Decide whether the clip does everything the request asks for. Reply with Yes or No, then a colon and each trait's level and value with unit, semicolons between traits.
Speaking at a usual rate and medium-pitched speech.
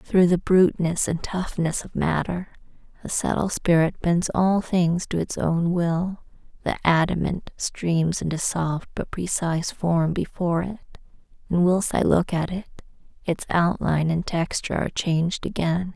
Yes: average, 150 wpm; medium, 175 Hz